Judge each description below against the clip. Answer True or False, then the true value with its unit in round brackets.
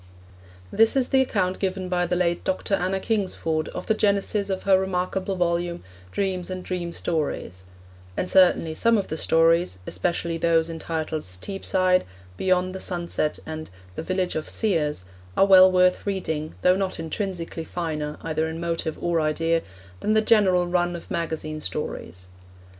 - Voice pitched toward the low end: False (175 Hz)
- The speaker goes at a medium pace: True (160 wpm)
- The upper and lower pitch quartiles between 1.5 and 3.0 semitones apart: True (2.7 semitones)